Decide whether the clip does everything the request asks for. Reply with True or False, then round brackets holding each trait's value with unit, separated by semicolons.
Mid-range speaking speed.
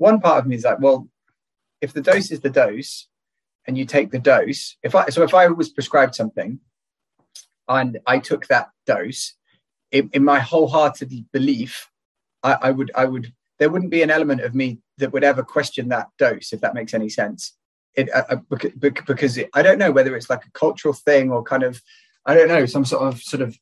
False (210 wpm)